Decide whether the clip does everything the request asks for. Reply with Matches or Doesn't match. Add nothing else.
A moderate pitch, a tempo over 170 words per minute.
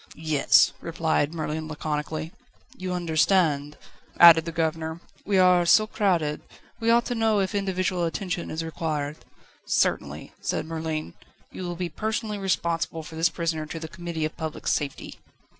Doesn't match